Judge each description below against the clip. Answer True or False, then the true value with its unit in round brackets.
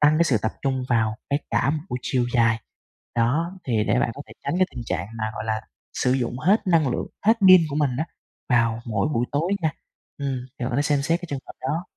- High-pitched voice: False (130 Hz)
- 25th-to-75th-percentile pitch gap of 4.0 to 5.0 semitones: True (4.7 semitones)